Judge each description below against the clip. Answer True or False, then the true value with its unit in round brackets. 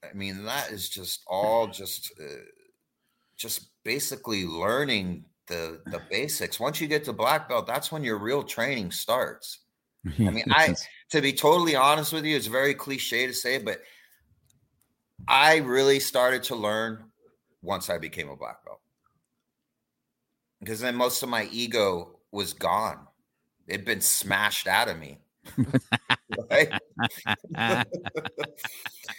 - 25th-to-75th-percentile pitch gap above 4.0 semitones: True (4.5 semitones)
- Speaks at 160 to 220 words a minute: False (135 wpm)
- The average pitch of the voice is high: False (125 Hz)